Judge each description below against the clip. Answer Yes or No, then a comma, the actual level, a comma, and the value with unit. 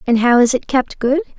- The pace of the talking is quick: Yes, fast, 260 wpm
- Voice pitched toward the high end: Yes, very high, 260 Hz